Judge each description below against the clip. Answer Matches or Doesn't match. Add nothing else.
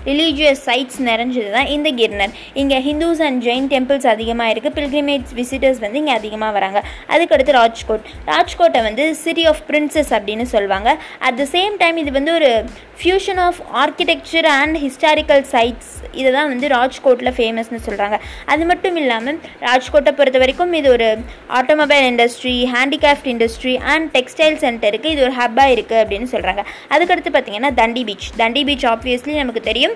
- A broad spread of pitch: Doesn't match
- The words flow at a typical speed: Doesn't match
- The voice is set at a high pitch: Matches